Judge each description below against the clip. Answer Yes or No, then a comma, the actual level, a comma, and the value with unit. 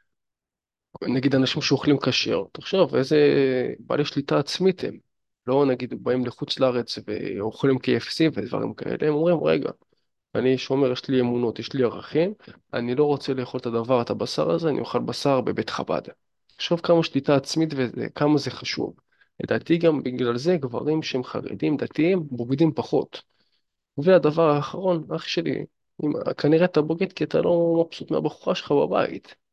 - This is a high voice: No, medium, 140 Hz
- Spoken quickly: Yes, fast, 160 wpm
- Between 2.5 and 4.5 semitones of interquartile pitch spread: Yes, average, 4.0 semitones